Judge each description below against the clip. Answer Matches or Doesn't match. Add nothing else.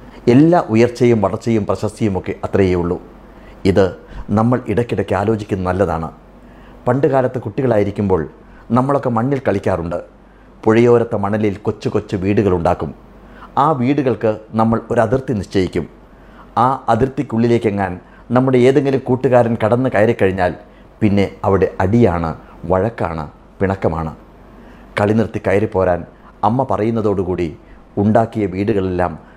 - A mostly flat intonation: Doesn't match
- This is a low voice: Matches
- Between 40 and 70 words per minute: Doesn't match